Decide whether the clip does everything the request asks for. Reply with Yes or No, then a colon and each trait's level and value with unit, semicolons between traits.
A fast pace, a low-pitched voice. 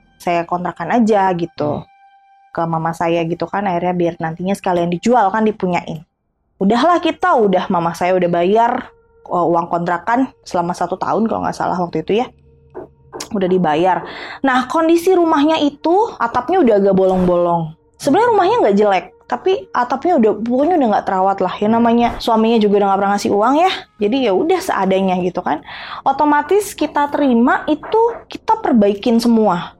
No: fast, 160 wpm; high, 210 Hz